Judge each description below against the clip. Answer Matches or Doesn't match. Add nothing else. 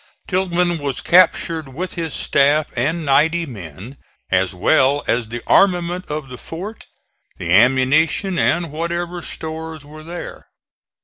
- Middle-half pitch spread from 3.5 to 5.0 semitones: Matches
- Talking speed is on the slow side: Matches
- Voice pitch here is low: Doesn't match